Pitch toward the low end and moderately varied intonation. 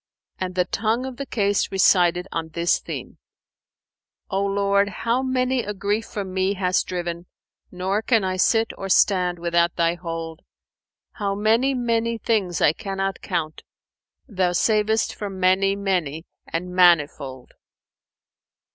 No: high, 195 Hz; average, 3.4 semitones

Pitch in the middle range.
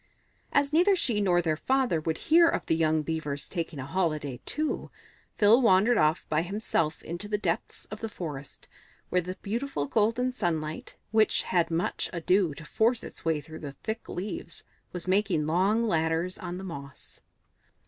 Yes: medium, 180 Hz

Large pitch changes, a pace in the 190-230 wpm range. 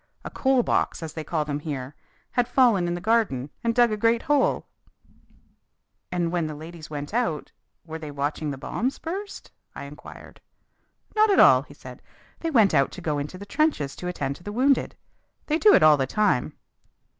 Yes: wide, 8.4 semitones; average, 200 wpm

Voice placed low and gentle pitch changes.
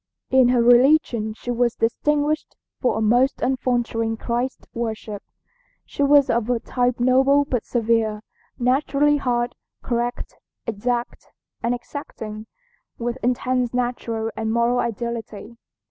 No: high, 240 Hz; narrow, 1.9 semitones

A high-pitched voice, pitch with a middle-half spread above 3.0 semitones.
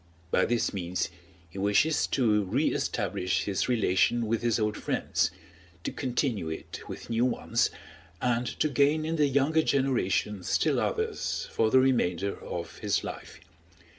No: low, 115 Hz; average, 5.2 semitones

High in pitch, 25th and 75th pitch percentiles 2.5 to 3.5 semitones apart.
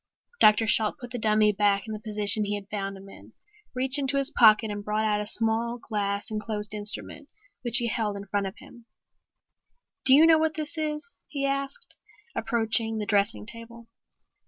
Yes: high, 220 Hz; average, 2.9 semitones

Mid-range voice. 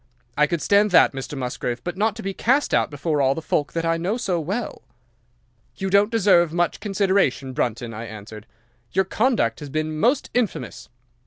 Yes: medium, 170 Hz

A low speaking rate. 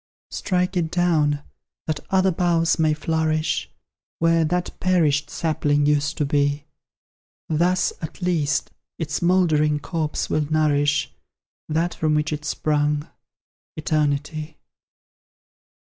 Yes: slow, 110 wpm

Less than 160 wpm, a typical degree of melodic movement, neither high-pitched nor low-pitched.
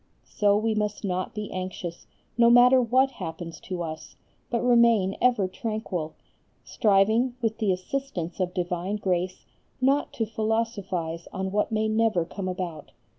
No: average, 145 wpm; average, 4.0 semitones; high, 205 Hz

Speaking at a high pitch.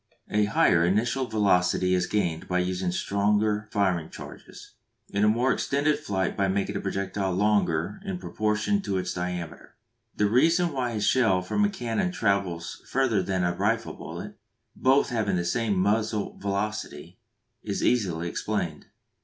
No: low, 100 Hz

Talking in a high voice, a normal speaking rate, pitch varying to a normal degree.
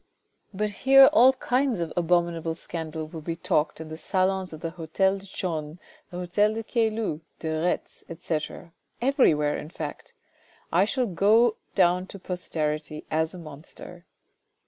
No: medium, 175 Hz; average, 150 wpm; average, 4.1 semitones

